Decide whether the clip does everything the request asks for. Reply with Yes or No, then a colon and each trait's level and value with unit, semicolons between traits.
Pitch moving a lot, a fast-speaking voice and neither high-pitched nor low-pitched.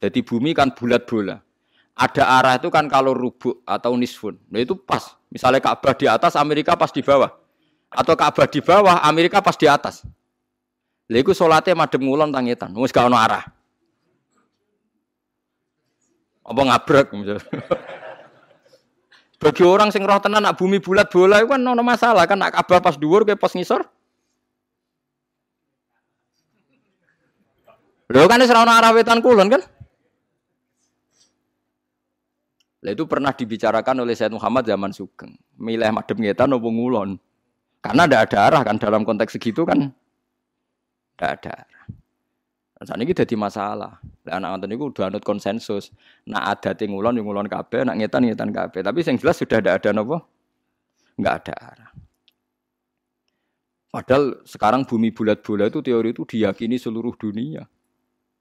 No: wide, 7.9 semitones; fast, 145 wpm; low, 130 Hz